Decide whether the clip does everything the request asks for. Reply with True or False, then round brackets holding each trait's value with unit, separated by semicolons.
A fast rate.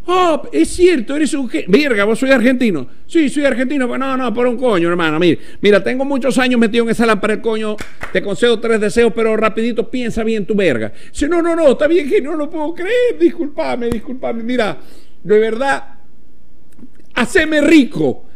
True (195 wpm)